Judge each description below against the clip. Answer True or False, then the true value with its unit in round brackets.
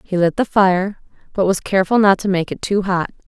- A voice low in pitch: False (190 Hz)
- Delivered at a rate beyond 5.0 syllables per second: True (5.5 syllables/s)